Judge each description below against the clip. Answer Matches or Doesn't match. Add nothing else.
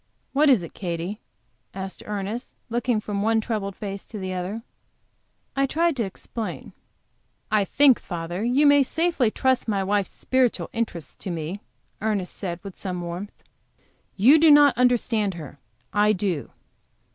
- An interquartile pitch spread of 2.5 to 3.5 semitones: Doesn't match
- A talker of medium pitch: Doesn't match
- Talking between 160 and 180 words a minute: Doesn't match